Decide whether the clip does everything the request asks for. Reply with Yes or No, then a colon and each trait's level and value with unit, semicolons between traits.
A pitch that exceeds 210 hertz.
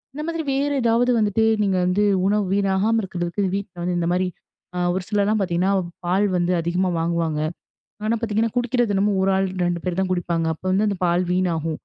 No: high, 190 Hz